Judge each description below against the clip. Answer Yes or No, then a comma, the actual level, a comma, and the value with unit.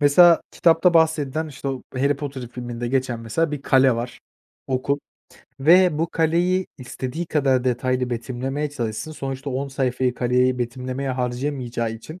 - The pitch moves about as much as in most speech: Yes, average, 3.1 semitones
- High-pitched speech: No, low, 135 Hz